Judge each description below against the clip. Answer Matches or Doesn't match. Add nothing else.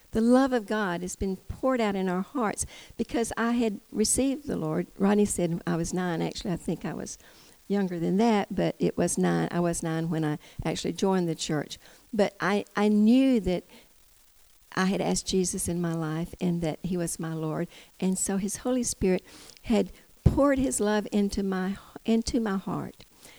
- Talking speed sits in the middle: Matches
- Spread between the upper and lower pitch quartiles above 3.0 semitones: Matches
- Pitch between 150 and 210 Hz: Matches